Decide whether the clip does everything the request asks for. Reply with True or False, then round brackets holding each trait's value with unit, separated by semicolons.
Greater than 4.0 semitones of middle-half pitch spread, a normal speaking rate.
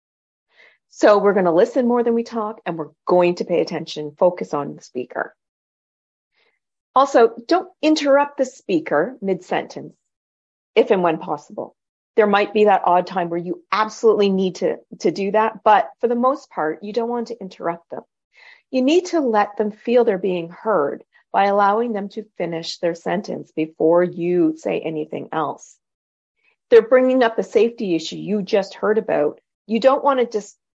True (5.4 semitones; 180 wpm)